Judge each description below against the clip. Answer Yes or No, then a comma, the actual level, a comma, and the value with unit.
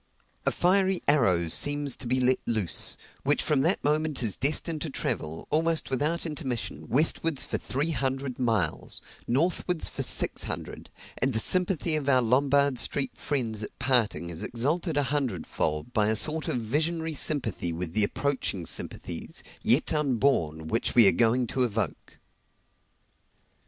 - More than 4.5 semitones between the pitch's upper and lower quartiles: Yes, average, 5.2 semitones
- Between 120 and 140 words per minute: No, average, 155 wpm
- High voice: No, low, 135 Hz